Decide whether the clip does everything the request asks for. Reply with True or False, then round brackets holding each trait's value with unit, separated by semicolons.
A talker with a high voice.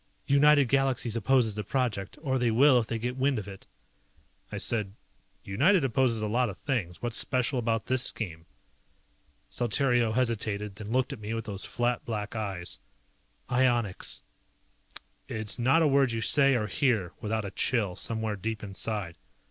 False (115 Hz)